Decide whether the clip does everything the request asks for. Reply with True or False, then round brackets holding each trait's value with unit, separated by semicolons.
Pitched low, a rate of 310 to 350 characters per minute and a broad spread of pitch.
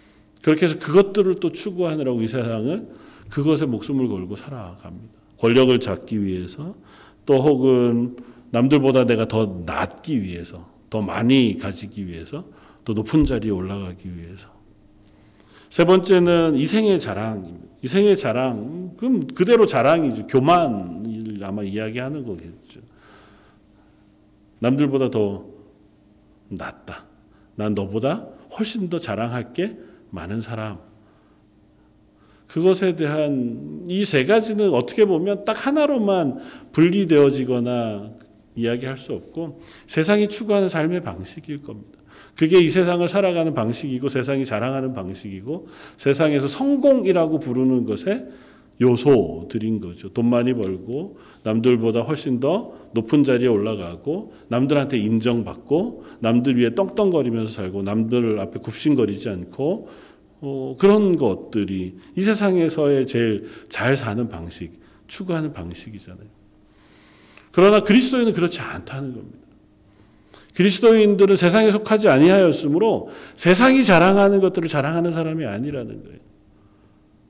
False (125 Hz; 290 characters per minute; 8.1 semitones)